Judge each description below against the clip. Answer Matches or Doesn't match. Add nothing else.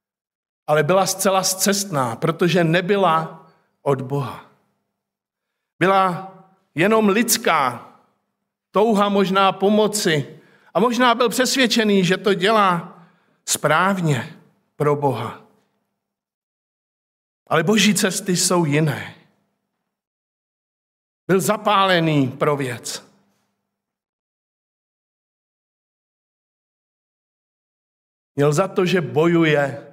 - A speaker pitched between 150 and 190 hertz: Matches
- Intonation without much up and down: Doesn't match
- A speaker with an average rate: Doesn't match